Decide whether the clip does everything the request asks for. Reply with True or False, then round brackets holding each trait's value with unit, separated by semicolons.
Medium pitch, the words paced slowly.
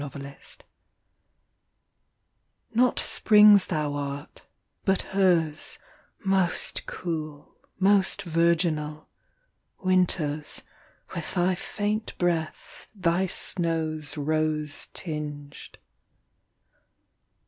True (165 Hz; 80 wpm)